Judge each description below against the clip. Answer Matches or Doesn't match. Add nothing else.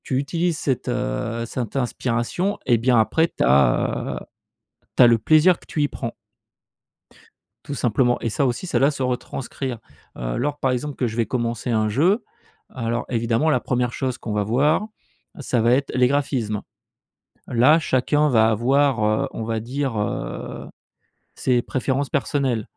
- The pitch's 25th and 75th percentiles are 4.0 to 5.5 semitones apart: Doesn't match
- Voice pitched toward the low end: Matches